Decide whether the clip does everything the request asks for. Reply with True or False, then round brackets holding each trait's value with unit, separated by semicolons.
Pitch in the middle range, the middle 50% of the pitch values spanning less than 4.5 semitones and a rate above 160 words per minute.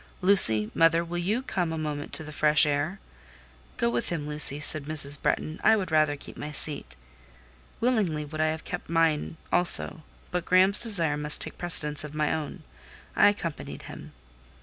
True (155 Hz; 2.9 semitones; 170 wpm)